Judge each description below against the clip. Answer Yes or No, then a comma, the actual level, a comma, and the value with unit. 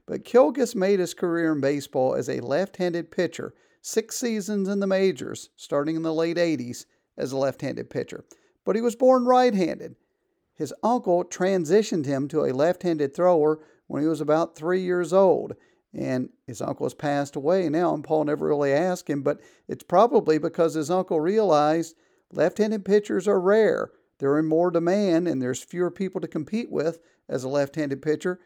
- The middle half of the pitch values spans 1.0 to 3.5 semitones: No, average, 4.2 semitones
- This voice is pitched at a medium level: Yes, medium, 170 Hz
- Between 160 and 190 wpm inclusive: Yes, average, 175 wpm